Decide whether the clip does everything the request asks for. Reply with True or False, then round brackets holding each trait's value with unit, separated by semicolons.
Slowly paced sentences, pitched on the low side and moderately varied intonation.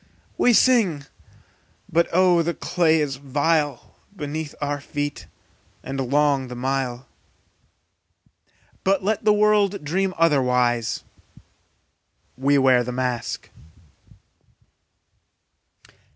False (95 wpm; 145 Hz; 4.9 semitones)